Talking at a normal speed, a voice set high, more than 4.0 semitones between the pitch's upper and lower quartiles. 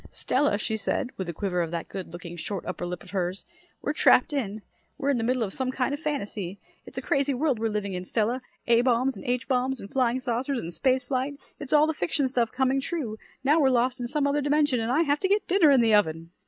No: fast, 250 wpm; very high, 250 Hz; average, 5.1 semitones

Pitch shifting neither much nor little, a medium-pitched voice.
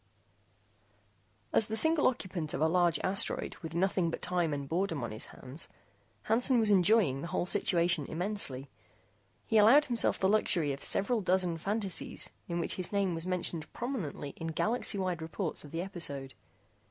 Yes: average, 4.2 semitones; medium, 180 Hz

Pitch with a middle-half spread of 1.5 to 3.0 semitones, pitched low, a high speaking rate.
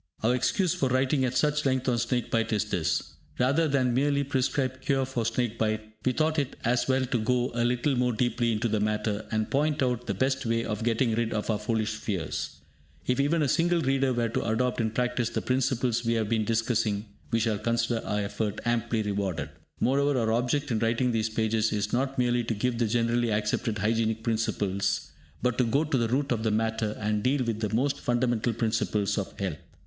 Yes: average, 2.7 semitones; low, 115 Hz; fast, 210 wpm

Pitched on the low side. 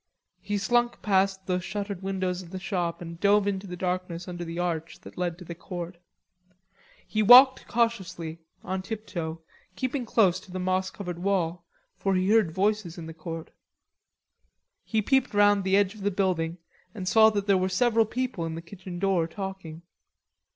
No: high, 190 Hz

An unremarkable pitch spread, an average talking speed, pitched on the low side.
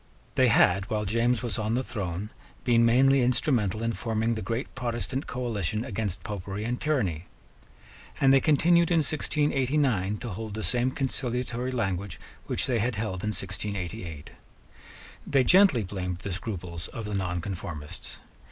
Yes: average, 4.5 semitones; average, 150 wpm; low, 115 Hz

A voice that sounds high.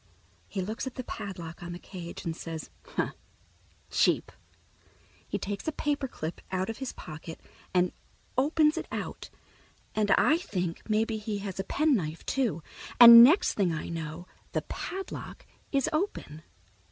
Yes: high, 205 Hz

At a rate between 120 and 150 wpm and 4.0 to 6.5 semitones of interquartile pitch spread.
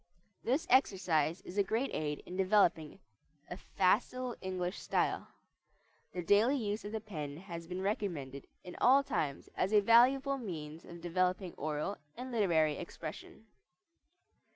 Yes: average, 140 wpm; average, 5.1 semitones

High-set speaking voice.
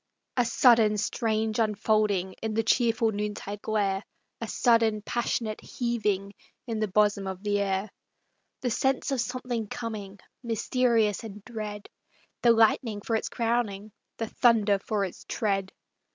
Yes: high, 215 Hz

